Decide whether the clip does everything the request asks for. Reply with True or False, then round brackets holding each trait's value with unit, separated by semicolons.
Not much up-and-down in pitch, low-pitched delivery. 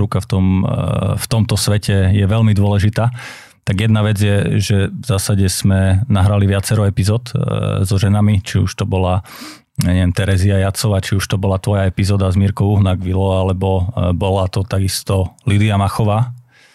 True (1.7 semitones; 100 Hz)